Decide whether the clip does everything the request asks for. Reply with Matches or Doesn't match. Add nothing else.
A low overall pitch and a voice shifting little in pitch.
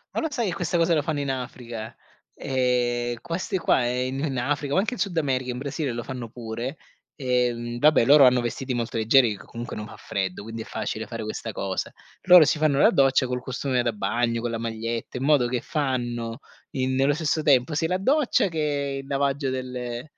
Doesn't match